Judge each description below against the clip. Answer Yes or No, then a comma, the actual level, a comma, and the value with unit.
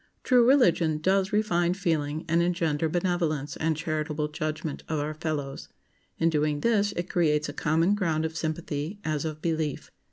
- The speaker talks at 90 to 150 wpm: No, average, 160 wpm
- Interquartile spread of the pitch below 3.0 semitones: Yes, narrow, 2.4 semitones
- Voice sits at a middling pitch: Yes, medium, 160 Hz